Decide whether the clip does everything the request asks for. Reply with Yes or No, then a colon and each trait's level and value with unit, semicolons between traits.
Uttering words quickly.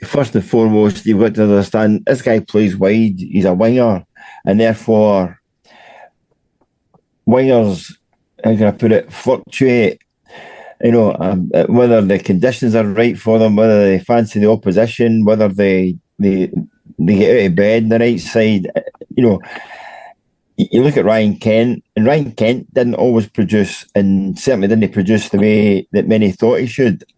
No: average, 165 wpm